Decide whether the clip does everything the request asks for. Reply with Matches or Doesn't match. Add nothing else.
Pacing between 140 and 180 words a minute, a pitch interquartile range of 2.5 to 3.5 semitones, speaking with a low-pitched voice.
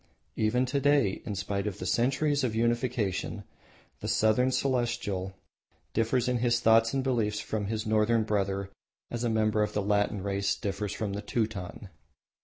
Matches